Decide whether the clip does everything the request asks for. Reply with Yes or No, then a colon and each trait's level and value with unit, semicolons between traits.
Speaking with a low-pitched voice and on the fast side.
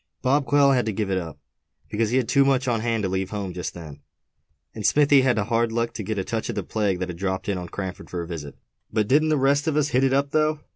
Yes: low, 115 Hz; fast, 285 wpm